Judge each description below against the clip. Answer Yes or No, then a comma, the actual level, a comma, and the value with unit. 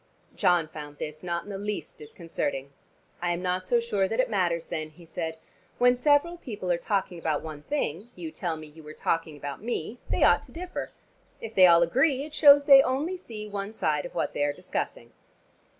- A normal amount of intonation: No, wide, 7.1 semitones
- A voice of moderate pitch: Yes, medium, 180 Hz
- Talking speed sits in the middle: No, fast, 210 wpm